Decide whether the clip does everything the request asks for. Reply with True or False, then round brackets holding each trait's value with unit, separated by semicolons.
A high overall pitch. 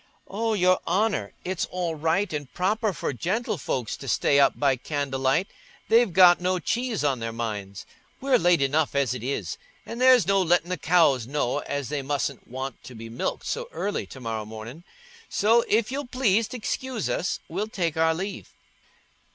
False (165 Hz)